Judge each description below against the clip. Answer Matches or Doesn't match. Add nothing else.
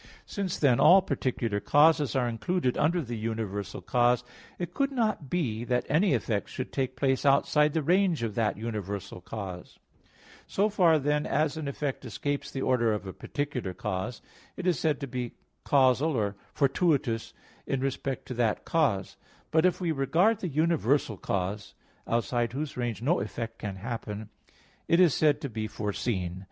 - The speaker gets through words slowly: Doesn't match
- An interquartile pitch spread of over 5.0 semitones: Matches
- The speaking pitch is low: Matches